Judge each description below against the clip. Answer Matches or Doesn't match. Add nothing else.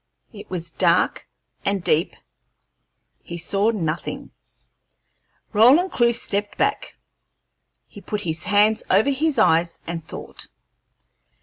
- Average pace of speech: Doesn't match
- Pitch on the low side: Doesn't match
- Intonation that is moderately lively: Matches